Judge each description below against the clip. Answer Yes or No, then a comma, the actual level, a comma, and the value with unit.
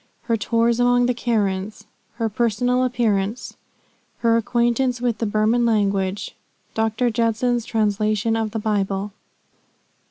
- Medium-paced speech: No, slow, 120 wpm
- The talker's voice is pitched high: Yes, high, 225 Hz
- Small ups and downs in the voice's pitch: Yes, narrow, 2.2 semitones